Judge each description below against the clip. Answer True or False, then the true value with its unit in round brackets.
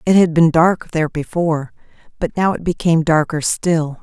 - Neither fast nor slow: True (180 wpm)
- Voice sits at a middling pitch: True (165 Hz)